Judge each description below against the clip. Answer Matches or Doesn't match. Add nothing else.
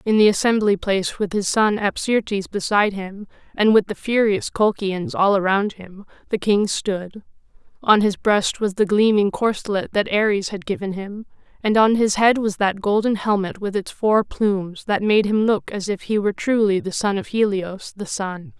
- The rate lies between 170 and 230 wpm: Matches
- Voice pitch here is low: Doesn't match